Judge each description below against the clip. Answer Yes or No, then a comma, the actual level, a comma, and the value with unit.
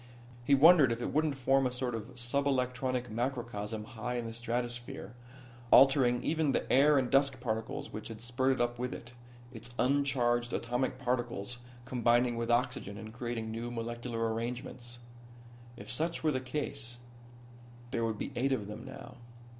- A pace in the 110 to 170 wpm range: Yes, average, 160 wpm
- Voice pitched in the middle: No, low, 120 Hz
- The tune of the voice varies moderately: No, narrow, 2.0 semitones